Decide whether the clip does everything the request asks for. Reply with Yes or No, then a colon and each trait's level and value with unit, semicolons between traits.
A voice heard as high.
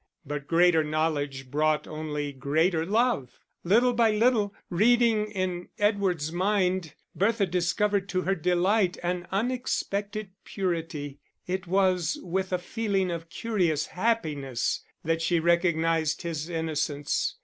No: medium, 175 Hz